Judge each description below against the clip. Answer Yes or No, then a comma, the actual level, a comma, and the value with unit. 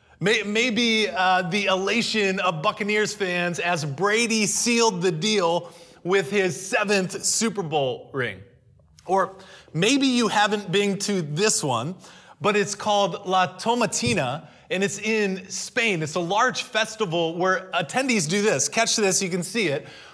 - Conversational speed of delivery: Yes, average, 145 wpm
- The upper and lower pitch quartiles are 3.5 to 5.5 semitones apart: No, average, 2.8 semitones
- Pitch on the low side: No, high, 195 Hz